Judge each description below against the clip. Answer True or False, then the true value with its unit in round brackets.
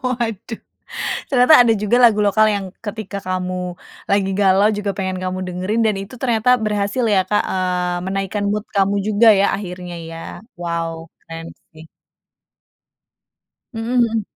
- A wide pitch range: False (2.8 semitones)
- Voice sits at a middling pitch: False (200 Hz)